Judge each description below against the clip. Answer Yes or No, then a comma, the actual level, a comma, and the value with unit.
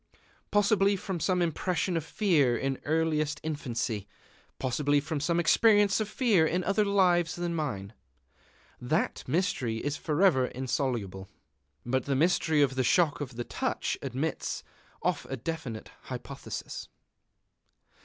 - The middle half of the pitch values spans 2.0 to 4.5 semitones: No, wide, 5.4 semitones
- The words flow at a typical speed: No, slow, 130 wpm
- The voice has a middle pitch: Yes, medium, 155 Hz